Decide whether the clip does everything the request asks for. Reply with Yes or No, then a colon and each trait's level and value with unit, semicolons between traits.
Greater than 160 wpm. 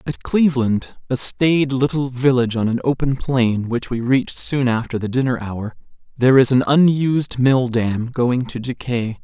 Yes: average, 175 wpm